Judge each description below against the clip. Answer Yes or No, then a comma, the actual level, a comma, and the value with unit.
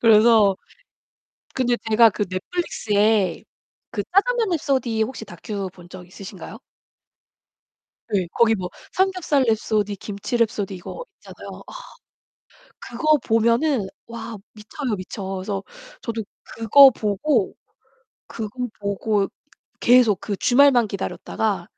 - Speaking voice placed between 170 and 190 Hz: No, high, 220 Hz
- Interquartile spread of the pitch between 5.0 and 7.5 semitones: No, average, 3.6 semitones